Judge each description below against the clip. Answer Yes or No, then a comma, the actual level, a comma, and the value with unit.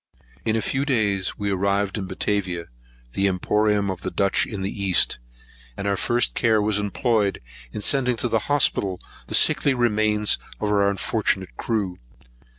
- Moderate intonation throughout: No, narrow, 2.2 semitones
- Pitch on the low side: Yes, low, 105 Hz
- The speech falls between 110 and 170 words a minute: Yes, average, 160 wpm